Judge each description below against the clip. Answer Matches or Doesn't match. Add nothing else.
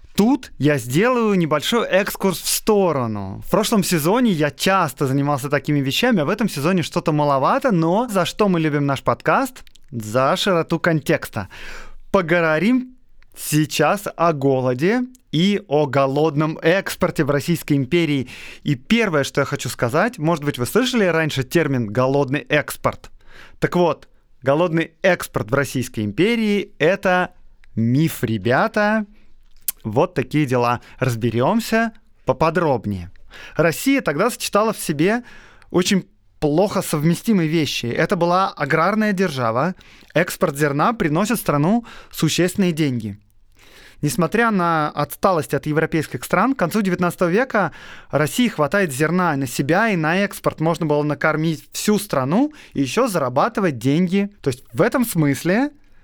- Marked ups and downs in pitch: Matches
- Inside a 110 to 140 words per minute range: Matches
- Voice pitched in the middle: Matches